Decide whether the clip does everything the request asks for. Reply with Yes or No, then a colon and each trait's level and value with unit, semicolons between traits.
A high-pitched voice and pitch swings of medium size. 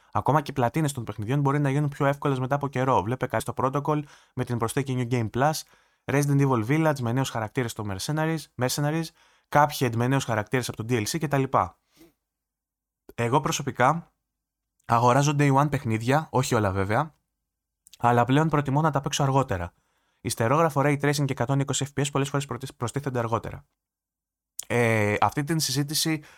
No: low, 130 Hz; average, 3.9 semitones